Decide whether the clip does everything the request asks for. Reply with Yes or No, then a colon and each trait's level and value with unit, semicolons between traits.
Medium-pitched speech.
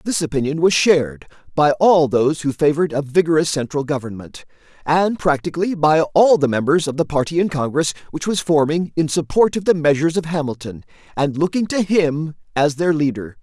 Yes: medium, 155 Hz